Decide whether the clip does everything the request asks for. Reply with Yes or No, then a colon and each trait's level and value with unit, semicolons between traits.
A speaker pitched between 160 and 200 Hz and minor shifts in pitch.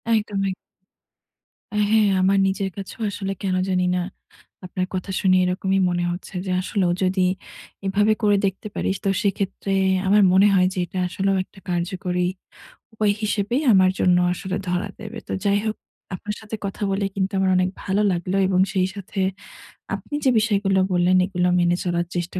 Yes: high, 190 Hz; narrow, 1.7 semitones